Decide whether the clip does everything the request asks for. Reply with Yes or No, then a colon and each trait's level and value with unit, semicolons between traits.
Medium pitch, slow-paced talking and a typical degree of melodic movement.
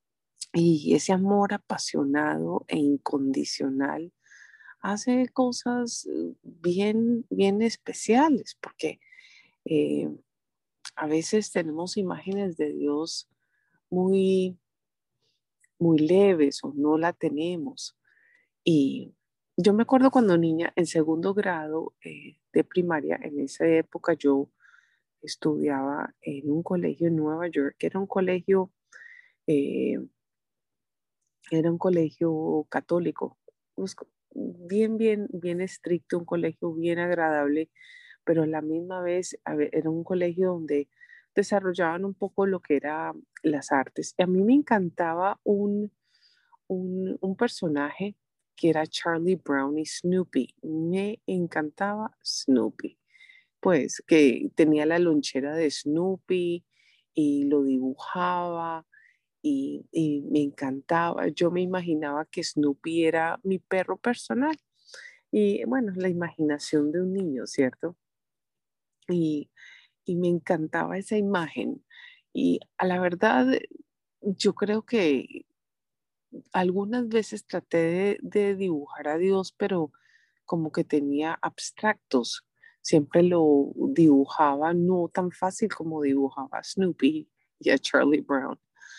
Yes: medium, 175 Hz; slow, 115 wpm; average, 4.5 semitones